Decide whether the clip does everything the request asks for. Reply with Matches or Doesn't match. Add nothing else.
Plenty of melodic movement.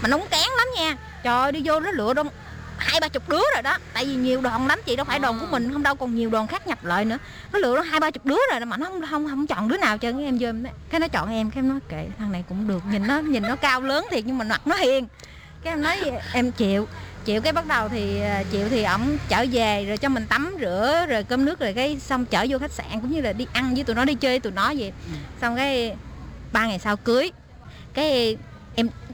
Doesn't match